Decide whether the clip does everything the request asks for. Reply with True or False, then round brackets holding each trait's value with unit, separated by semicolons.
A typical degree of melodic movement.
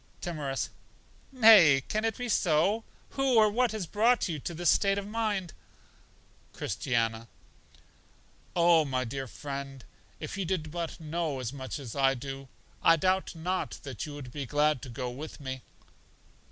False (6.2 semitones)